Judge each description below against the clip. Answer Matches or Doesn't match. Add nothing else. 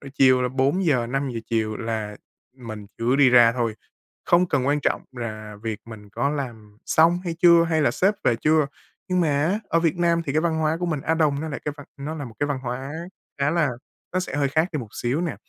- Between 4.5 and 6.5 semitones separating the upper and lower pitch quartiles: Matches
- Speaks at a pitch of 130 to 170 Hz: Matches